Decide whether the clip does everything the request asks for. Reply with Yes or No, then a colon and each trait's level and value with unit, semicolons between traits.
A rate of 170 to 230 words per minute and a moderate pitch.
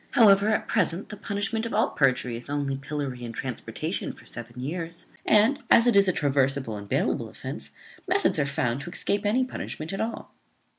Yes: average, 190 wpm; medium, 160 Hz